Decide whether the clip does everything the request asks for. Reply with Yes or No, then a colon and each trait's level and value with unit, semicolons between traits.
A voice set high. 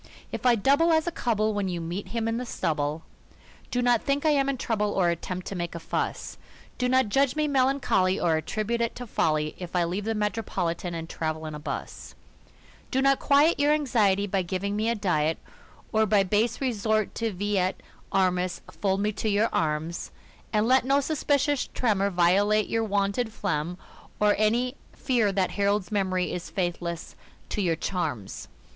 Yes: high, 205 Hz